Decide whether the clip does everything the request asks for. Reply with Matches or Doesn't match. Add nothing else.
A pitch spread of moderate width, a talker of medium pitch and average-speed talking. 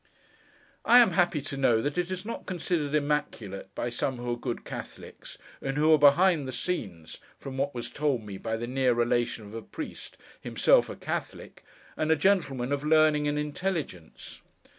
Matches